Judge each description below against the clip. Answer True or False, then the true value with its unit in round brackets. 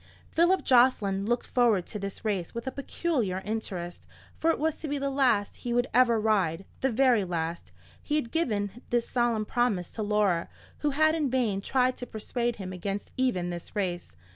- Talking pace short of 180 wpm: False (185 wpm)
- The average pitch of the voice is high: True (230 Hz)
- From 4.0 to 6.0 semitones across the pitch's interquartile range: True (4.8 semitones)